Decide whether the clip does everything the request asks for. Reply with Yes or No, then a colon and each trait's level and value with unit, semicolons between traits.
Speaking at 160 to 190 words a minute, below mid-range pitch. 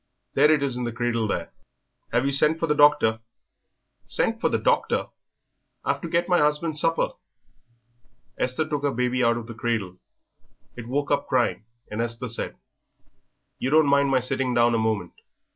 Yes: average, 175 wpm; low, 130 Hz